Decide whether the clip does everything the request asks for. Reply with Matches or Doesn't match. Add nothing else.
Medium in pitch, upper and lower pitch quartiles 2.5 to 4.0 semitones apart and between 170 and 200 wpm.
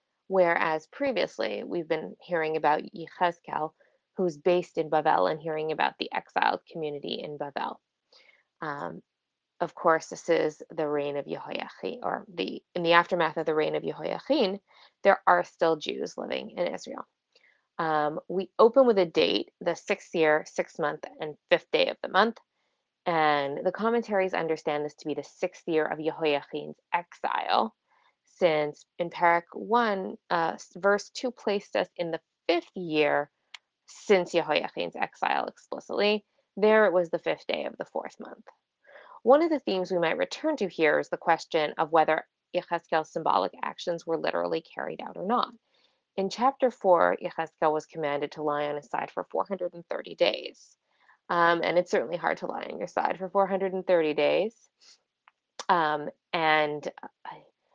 Doesn't match